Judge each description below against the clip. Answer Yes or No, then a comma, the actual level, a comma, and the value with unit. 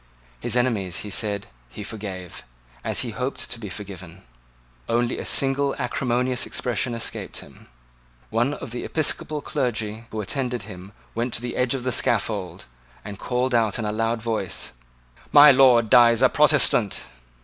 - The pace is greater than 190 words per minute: No, average, 160 wpm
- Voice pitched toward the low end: Yes, low, 115 Hz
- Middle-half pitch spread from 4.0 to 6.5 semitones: No, average, 3.2 semitones